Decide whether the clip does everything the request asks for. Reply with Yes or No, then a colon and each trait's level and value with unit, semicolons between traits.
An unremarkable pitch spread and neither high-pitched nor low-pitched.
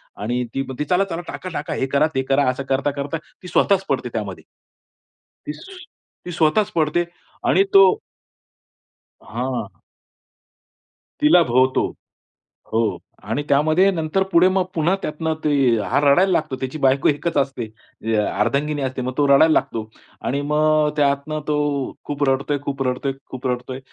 Yes: average, 3.4 semitones; medium, 145 Hz